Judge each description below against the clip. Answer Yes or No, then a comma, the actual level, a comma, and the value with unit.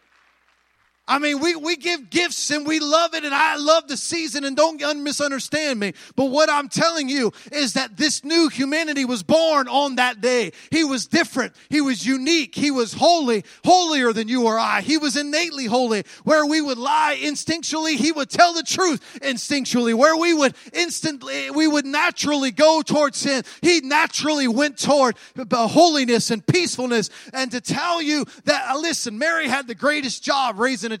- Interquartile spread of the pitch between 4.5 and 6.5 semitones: No, average, 3.6 semitones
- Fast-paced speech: No, average, 180 wpm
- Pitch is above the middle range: Yes, very high, 290 Hz